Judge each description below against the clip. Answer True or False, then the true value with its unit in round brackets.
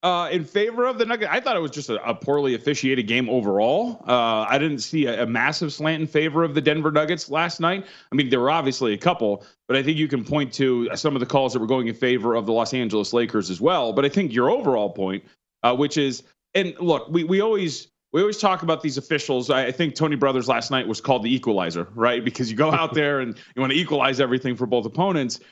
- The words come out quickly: True (255 wpm)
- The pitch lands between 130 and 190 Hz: True (140 Hz)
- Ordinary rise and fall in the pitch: True (4.4 semitones)